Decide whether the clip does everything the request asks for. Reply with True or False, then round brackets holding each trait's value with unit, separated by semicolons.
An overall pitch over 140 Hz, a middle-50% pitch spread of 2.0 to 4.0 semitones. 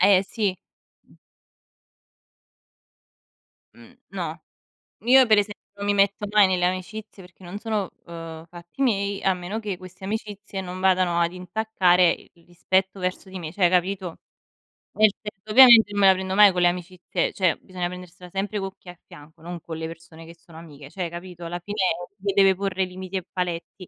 True (185 Hz; 2.4 semitones)